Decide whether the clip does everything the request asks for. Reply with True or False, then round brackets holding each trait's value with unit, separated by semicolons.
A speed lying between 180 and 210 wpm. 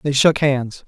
True (205 wpm)